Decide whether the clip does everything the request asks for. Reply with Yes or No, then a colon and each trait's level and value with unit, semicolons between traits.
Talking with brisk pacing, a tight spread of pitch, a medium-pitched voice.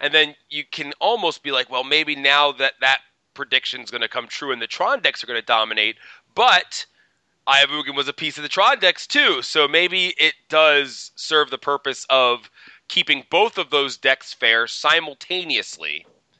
No: average, 185 wpm; narrow, 2.3 semitones; medium, 150 Hz